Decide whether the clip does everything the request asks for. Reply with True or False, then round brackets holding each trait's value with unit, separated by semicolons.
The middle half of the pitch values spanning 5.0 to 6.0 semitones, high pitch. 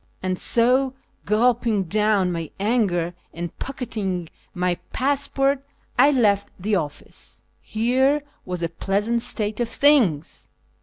True (5.6 semitones; 215 Hz)